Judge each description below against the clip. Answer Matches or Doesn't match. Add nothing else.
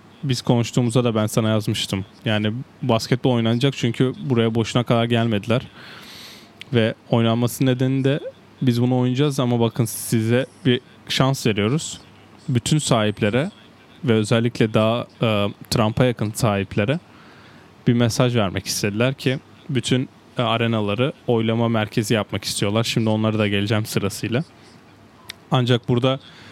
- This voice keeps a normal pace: Matches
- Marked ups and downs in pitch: Doesn't match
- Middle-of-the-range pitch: Doesn't match